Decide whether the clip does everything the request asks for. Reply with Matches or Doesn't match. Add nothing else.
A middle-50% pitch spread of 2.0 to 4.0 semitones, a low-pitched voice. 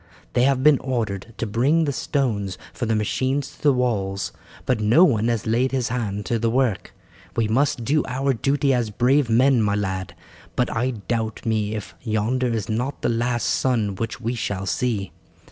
Matches